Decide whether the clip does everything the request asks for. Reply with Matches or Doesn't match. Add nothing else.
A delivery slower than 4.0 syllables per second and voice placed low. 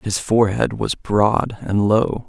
Matches